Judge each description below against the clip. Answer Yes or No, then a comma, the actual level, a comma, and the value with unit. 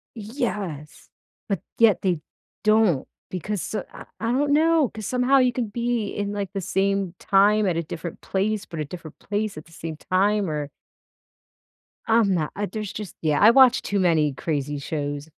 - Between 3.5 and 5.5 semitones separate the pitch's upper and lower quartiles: Yes, average, 4.7 semitones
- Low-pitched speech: No, high, 200 Hz